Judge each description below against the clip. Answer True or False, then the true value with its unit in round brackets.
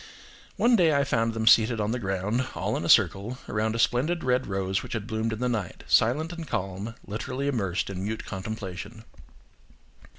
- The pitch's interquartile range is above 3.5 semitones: True (4.1 semitones)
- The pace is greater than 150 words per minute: True (190 wpm)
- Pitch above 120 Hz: False (110 Hz)